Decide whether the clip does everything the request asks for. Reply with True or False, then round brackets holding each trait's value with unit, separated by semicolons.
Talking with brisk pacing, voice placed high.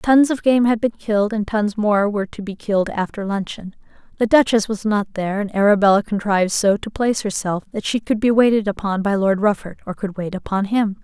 True (225 wpm; 210 Hz)